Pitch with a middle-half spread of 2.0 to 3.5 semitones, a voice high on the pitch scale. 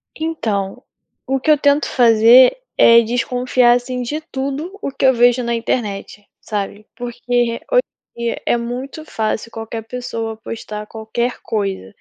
Yes: average, 2.7 semitones; high, 240 Hz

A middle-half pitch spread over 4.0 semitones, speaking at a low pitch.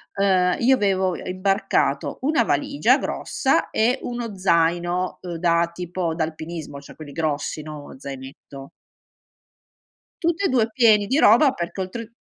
No: average, 5.2 semitones; medium, 180 Hz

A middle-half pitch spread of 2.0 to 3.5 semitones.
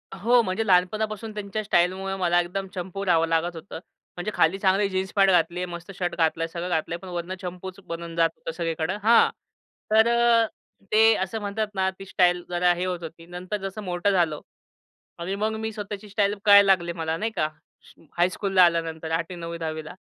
Yes: average, 3.0 semitones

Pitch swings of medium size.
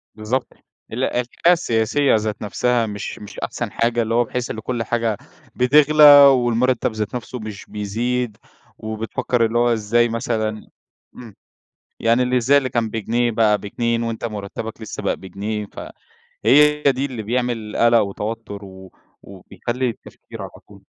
No: narrow, 2.3 semitones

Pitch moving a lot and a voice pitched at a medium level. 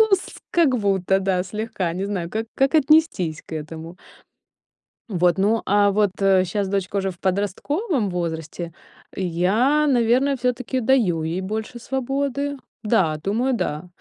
No: wide, 5.9 semitones; high, 205 Hz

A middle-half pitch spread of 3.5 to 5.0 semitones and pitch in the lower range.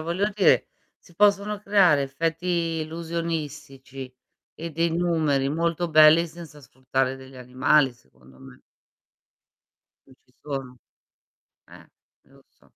No: average, 4.1 semitones; medium, 155 Hz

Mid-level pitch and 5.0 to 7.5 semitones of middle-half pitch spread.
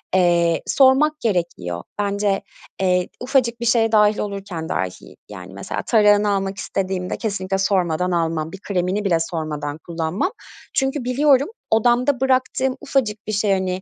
No: high, 195 Hz; average, 5.3 semitones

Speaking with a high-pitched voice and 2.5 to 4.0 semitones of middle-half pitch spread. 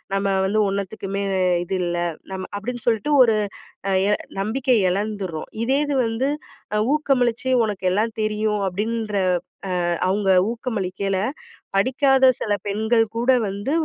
Yes: high, 215 Hz; average, 3.4 semitones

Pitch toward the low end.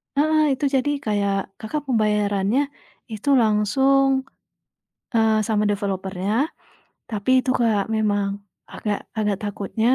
No: high, 210 Hz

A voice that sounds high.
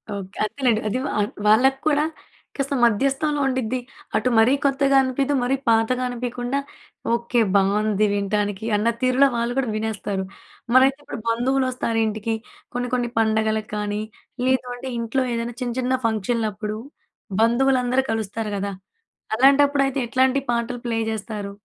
Yes: high, 235 Hz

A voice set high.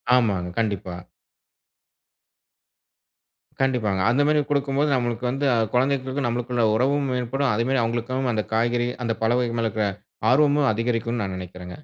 No: low, 120 Hz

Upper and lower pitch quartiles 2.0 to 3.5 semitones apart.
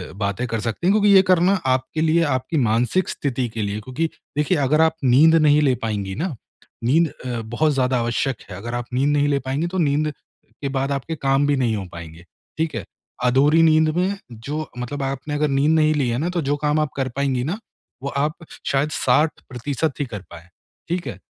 No: average, 4.1 semitones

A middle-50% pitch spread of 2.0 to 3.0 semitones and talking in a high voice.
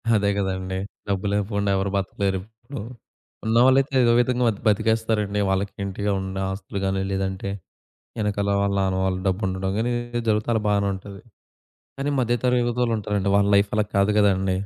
No: narrow, 2.6 semitones; low, 100 Hz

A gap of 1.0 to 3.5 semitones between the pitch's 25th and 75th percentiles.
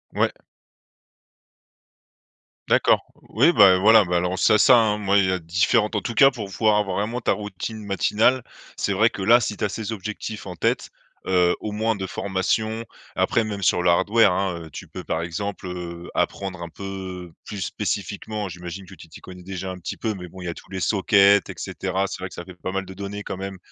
Yes: average, 2.7 semitones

